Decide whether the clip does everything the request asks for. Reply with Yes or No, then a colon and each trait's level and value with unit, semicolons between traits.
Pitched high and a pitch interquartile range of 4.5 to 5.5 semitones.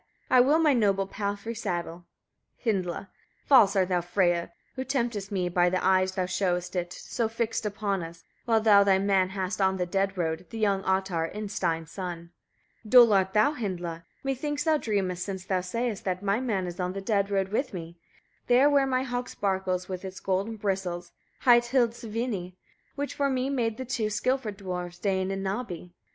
No: high, 195 Hz; average, 4.0 semitones